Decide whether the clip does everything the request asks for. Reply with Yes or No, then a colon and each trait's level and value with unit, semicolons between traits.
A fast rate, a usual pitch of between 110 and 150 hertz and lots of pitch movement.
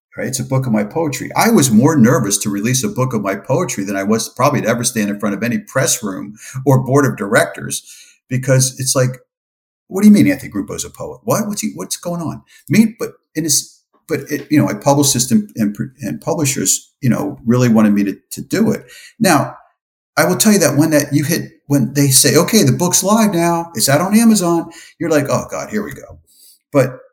Yes: fast, 235 wpm; medium, 140 Hz; wide, 6.2 semitones